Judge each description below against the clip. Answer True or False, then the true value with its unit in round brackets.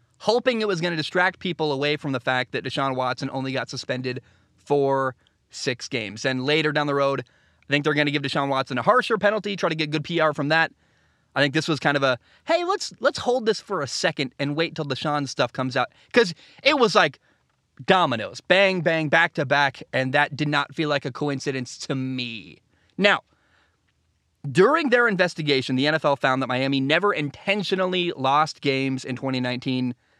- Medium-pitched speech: True (145 Hz)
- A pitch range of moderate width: True (4.0 semitones)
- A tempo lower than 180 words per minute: False (195 wpm)